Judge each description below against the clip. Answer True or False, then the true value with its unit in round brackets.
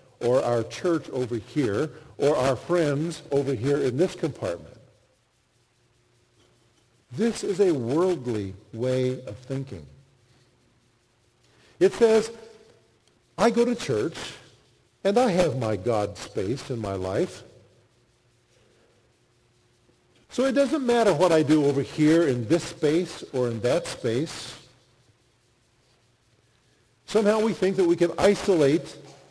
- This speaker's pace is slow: True (120 wpm)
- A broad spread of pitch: True (6.9 semitones)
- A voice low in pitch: True (130 Hz)